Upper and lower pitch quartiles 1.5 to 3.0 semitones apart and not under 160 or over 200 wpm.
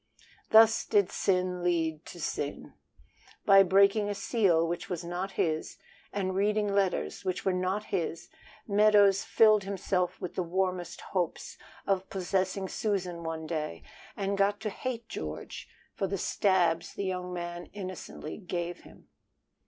No: narrow, 2.4 semitones; average, 145 wpm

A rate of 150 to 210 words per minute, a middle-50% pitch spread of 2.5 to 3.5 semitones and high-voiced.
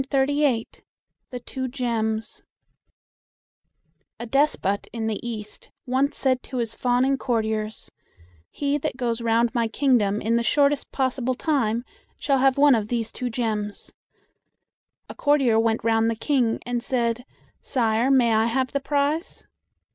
No: average, 140 wpm; average, 3.2 semitones; high, 240 Hz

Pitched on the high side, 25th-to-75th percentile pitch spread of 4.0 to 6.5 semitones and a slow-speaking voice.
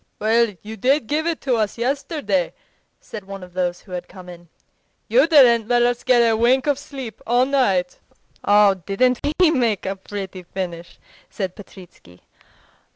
No: high, 220 Hz; average, 5.1 semitones; average, 165 wpm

